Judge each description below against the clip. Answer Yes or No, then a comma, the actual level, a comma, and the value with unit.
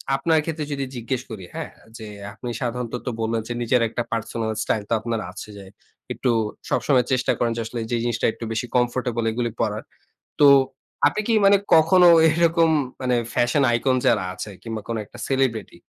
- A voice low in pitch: Yes, low, 120 Hz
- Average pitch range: Yes, average, 3.1 semitones